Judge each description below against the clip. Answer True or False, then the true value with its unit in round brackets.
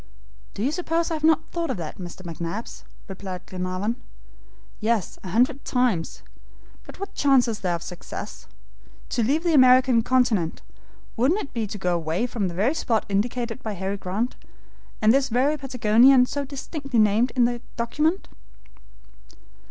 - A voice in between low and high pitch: False (235 Hz)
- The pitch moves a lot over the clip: True (5.7 semitones)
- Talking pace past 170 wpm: False (165 wpm)